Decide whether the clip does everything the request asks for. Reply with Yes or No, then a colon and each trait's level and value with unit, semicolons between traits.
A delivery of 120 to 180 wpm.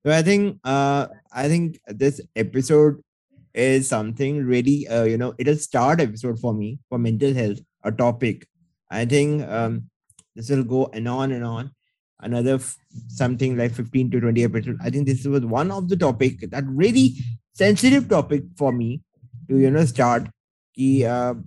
Yes: average, 170 wpm